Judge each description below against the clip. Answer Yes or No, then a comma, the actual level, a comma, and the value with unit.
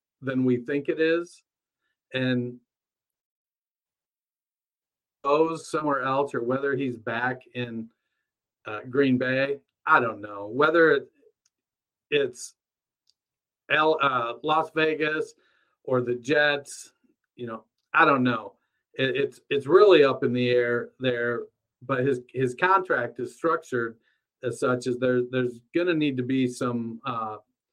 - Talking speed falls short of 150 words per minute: Yes, slow, 135 wpm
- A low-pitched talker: Yes, low, 130 Hz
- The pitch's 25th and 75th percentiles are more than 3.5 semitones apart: Yes, average, 4.2 semitones